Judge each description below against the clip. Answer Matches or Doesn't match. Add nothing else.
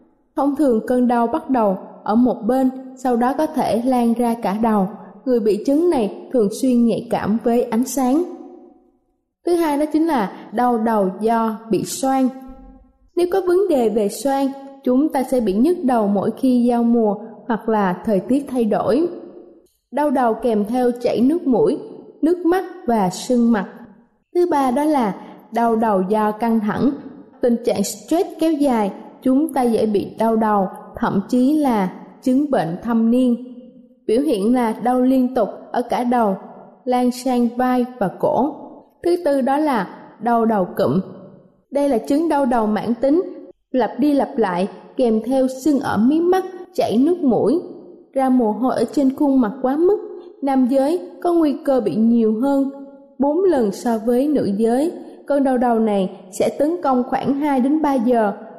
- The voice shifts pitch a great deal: Doesn't match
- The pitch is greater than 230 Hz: Matches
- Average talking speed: Matches